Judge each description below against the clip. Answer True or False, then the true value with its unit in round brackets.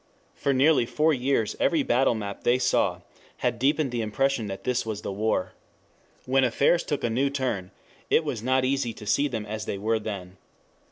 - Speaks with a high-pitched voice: False (120 Hz)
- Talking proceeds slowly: False (190 wpm)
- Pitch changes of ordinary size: True (4.1 semitones)